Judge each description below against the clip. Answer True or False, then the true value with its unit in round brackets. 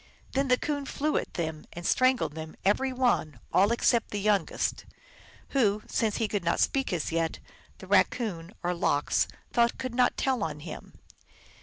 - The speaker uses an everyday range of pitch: False (7.3 semitones)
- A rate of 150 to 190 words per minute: True (170 wpm)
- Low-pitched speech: False (210 Hz)